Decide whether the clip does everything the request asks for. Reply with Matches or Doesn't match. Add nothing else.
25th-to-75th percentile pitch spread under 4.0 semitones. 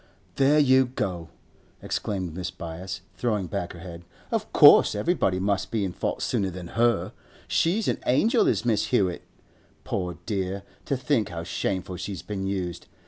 Doesn't match